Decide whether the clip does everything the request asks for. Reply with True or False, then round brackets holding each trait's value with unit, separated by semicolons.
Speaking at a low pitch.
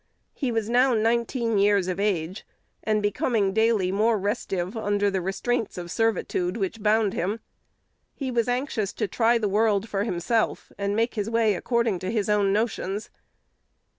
False (210 Hz)